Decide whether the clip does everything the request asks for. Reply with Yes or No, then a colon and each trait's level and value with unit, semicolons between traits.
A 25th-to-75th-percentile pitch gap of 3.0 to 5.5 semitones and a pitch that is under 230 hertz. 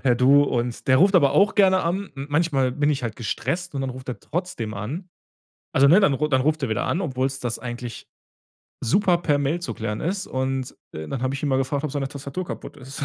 Yes: average, 4.5 semitones; medium, 140 Hz